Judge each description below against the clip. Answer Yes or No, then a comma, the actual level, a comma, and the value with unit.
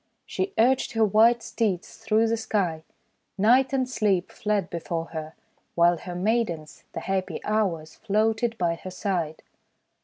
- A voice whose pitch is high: Yes, high, 205 Hz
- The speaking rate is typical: Yes, average, 145 wpm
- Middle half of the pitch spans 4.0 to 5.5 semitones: Yes, average, 4.6 semitones